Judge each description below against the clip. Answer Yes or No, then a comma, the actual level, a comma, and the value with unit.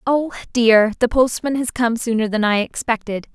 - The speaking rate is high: No, average, 180 wpm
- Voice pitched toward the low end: No, high, 235 Hz